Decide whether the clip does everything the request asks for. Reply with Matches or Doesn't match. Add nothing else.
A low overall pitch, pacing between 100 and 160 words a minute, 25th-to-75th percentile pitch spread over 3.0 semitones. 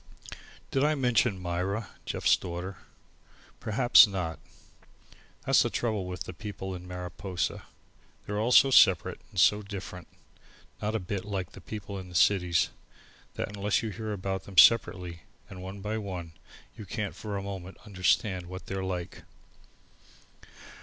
Doesn't match